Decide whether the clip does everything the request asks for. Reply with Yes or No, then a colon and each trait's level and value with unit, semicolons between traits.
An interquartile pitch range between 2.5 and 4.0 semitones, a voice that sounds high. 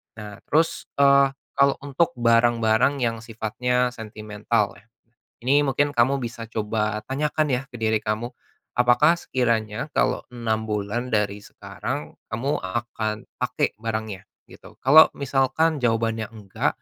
No: average, 3.6 semitones; low, 115 Hz